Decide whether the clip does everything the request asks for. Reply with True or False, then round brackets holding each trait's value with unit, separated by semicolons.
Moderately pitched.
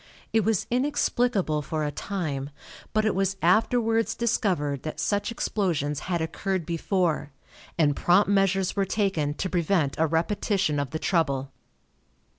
True (180 Hz)